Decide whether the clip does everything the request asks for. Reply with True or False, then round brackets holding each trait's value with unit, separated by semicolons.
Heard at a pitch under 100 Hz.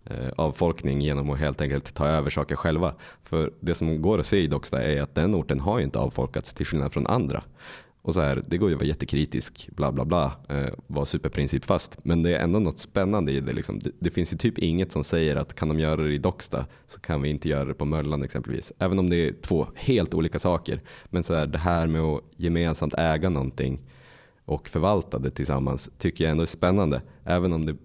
True (80 Hz)